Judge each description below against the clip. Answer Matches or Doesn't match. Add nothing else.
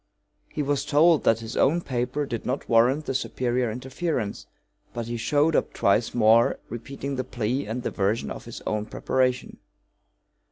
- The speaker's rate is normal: Matches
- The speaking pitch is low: Matches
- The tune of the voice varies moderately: Matches